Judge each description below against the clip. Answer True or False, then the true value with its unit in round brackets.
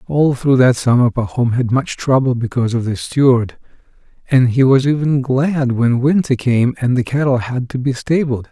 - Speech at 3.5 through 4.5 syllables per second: False (4.9 syllables/s)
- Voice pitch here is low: True (130 Hz)